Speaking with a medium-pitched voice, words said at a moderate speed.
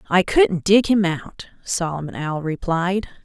Yes: medium, 180 Hz; average, 150 wpm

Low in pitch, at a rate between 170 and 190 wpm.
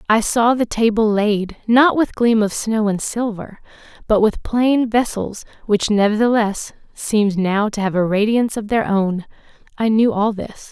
No: high, 215 Hz; average, 175 wpm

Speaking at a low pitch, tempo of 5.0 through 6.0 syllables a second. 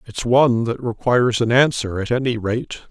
Yes: low, 120 Hz; 5.4 syllables/s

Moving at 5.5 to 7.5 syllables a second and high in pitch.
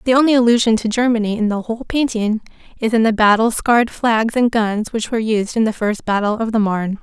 Yes: 6.0 syllables/s; high, 225 Hz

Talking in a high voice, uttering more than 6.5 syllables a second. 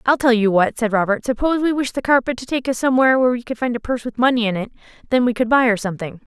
Yes: high, 240 Hz; 7.5 syllables/s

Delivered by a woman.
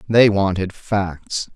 No: male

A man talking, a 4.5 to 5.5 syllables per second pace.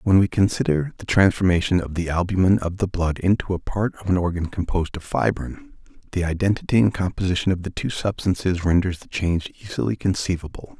No: male; 6.0 syllables/s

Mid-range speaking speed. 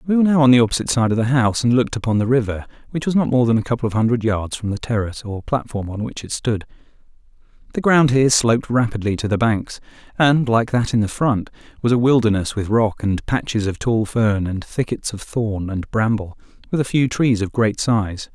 No: fast, 230 wpm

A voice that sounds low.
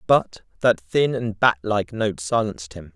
Yes: low, 105 Hz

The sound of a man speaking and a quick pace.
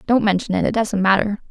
No: female; fast, 240 wpm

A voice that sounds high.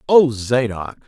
No: low, 120 Hz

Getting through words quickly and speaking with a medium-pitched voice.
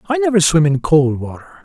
Yes: fast, 220 wpm; medium, 175 Hz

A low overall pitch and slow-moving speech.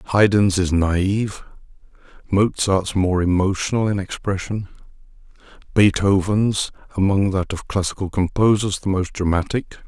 Yes: very low, 95 Hz; slow, 105 wpm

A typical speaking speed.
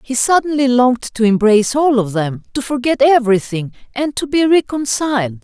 Yes: average, 165 wpm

